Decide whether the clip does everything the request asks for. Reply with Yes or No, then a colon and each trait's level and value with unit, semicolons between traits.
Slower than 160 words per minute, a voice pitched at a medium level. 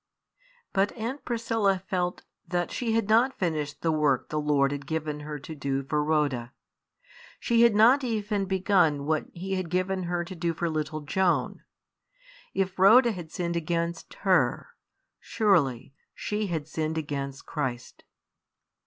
Yes: average, 150 wpm; medium, 170 Hz